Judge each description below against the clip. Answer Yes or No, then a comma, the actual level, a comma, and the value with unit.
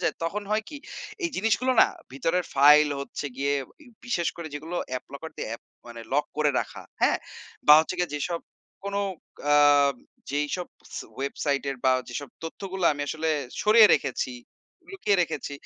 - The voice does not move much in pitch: No, average, 5.0 semitones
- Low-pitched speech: No, medium, 160 Hz